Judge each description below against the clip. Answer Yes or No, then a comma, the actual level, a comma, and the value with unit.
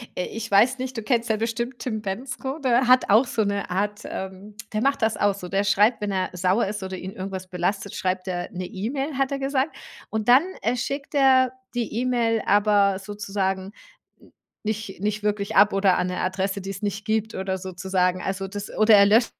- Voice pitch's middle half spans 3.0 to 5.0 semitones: Yes, average, 3.6 semitones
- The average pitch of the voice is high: Yes, high, 205 Hz